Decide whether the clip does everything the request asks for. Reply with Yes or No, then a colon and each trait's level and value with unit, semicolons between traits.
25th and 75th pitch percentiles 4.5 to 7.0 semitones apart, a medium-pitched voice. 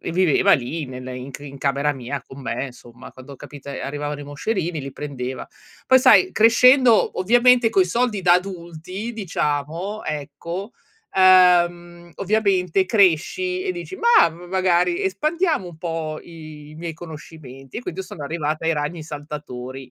Yes: average, 5.0 semitones; medium, 170 Hz